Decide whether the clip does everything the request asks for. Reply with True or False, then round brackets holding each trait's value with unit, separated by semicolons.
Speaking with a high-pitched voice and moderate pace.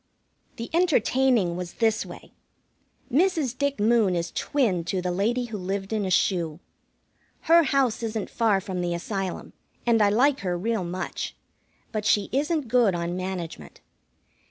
True (215 Hz; 155 wpm)